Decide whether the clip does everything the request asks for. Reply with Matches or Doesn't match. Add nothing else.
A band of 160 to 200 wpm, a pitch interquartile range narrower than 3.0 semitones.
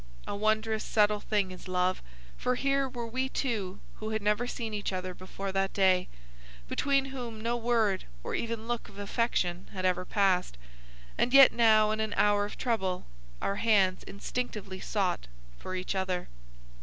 Doesn't match